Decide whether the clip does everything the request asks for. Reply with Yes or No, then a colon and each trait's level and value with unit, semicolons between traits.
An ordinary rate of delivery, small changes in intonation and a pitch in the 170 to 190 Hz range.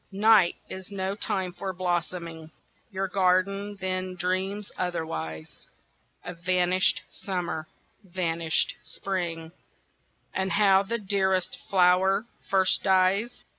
No: slow, 100 wpm; narrow, 1.6 semitones; medium, 185 Hz